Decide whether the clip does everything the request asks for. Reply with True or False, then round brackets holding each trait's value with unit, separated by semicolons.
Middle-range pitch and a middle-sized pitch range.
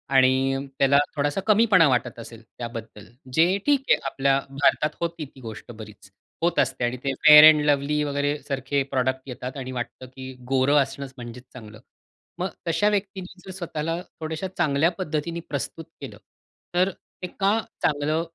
True (145 Hz; 4.2 semitones)